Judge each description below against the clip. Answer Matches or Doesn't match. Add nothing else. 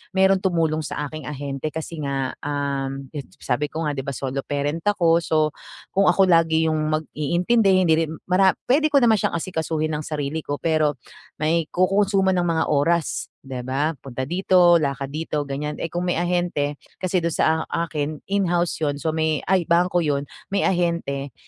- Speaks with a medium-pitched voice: Matches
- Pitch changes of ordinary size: Matches